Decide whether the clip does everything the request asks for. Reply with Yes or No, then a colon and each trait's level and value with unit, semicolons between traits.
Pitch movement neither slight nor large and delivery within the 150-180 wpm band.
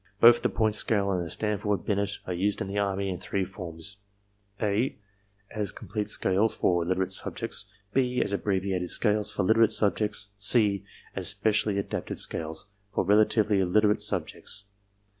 No: narrow, 2.0 semitones; average, 155 wpm